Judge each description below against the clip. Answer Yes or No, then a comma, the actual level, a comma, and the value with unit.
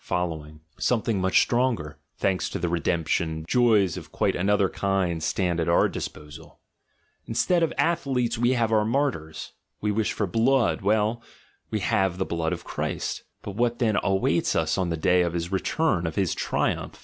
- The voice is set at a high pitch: No, very low, 95 Hz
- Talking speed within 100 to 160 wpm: No, average, 180 wpm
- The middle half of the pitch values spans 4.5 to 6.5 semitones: Yes, average, 5.2 semitones